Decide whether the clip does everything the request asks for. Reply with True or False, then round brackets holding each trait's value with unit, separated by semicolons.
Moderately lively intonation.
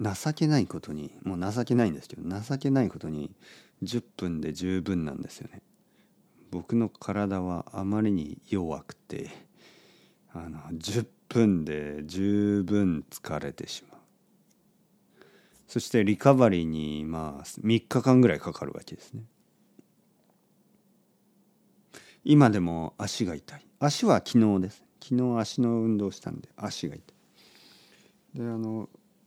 False (7.2 semitones)